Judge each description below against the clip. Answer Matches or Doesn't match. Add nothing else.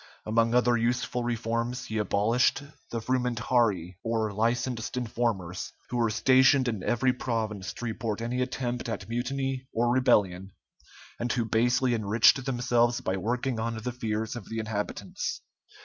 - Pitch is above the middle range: Doesn't match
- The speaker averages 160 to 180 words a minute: Doesn't match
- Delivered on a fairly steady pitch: Matches